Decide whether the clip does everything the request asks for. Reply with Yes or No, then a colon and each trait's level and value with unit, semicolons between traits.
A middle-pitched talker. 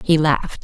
Yes: medium, 150 Hz